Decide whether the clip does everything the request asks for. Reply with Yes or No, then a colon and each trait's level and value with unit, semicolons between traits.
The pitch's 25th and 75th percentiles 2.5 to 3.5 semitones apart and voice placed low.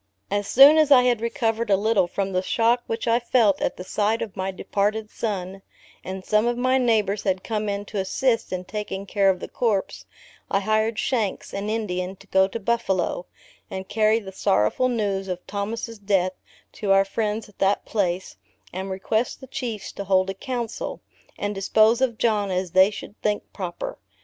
No: average, 2.9 semitones; high, 205 Hz